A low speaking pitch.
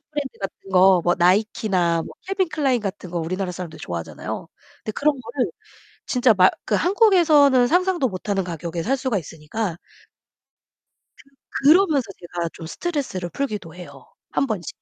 No: high, 205 Hz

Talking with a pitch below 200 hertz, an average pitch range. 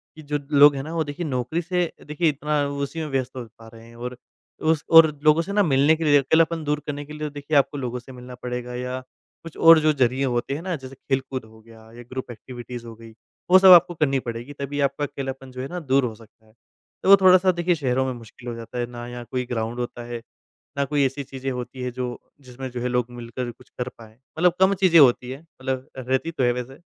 Yes: low, 135 Hz; average, 3.6 semitones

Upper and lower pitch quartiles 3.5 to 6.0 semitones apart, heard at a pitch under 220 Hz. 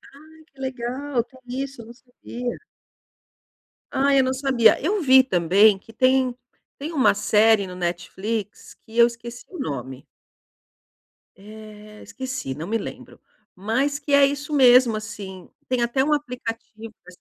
No: average, 4.1 semitones; high, 240 Hz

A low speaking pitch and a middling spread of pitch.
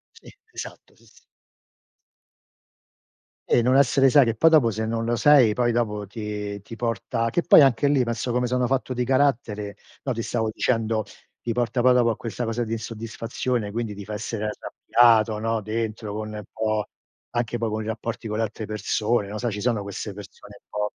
No: low, 115 Hz; narrow, 2.2 semitones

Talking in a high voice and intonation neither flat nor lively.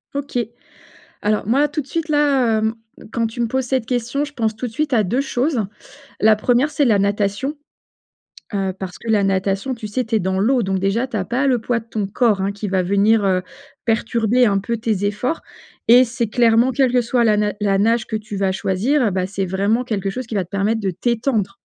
Yes: high, 225 Hz; average, 3.8 semitones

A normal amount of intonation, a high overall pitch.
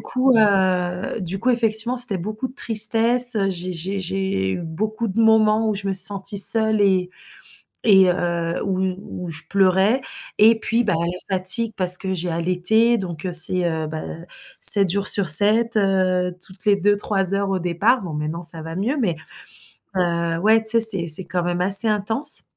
Yes: average, 3.6 semitones; high, 195 Hz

